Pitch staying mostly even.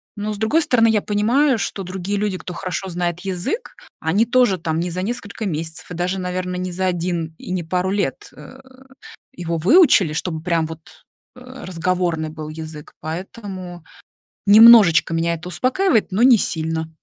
No: average, 4.1 semitones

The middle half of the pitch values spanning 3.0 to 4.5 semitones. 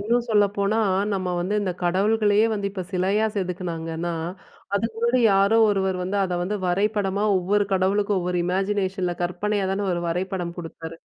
No: narrow, 2.4 semitones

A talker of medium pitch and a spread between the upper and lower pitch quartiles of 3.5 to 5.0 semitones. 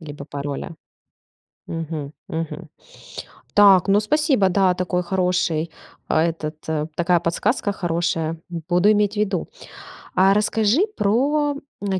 Yes: medium, 180 Hz; average, 3.9 semitones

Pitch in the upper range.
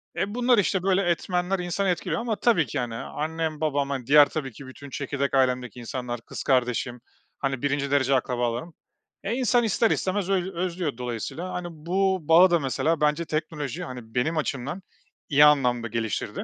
No: medium, 150 Hz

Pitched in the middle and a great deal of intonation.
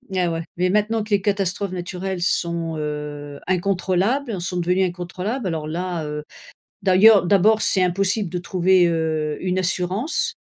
No: medium, 180 Hz; narrow, 2.6 semitones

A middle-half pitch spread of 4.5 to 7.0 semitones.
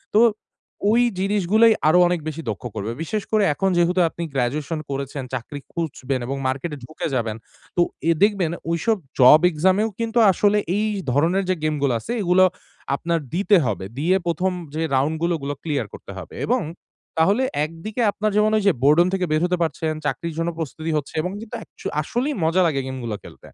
Yes: wide, 5.4 semitones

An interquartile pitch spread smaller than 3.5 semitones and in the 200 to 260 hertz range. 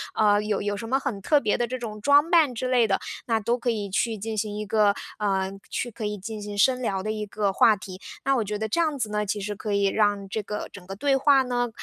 Yes: average, 3.0 semitones; high, 215 Hz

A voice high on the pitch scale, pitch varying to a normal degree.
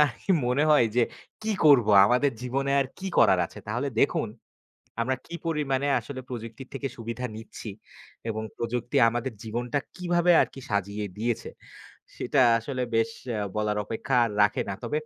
No: low, 125 Hz; average, 3.5 semitones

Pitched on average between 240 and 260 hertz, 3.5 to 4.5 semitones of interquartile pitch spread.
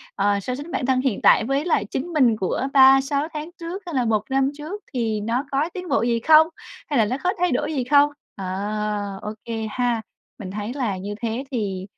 No: very high, 250 Hz; average, 5.3 semitones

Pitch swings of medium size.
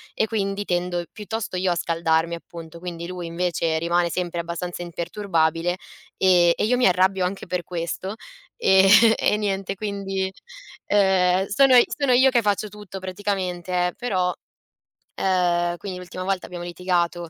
No: narrow, 2.3 semitones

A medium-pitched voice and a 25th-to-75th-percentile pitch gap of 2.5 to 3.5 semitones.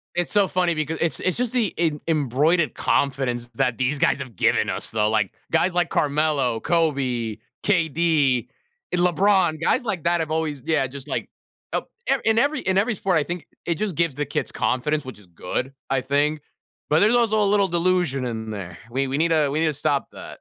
No: medium, 155 Hz; average, 4.7 semitones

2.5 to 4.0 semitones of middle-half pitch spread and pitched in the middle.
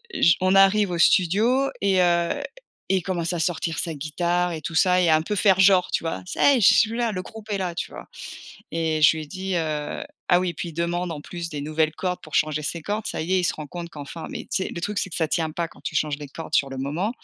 Yes: average, 3.1 semitones; medium, 175 Hz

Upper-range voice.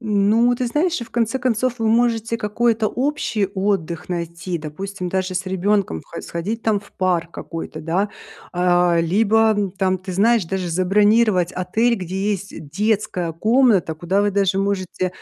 Yes: high, 200 Hz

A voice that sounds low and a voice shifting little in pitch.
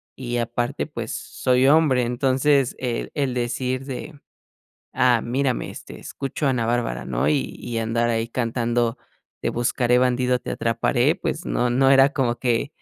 Yes: low, 125 Hz; narrow, 2.0 semitones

